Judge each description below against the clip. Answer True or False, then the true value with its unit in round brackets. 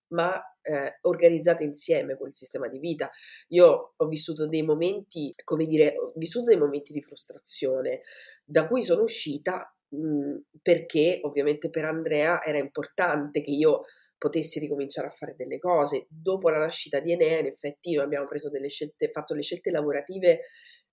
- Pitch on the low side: False (155 Hz)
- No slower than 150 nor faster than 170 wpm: True (160 wpm)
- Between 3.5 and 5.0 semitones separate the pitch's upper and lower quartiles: True (3.8 semitones)